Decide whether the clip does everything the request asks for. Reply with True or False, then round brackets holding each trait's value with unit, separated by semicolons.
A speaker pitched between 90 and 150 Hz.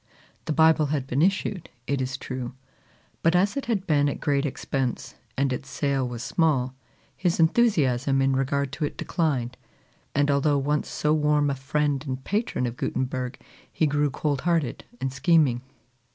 True (140 Hz)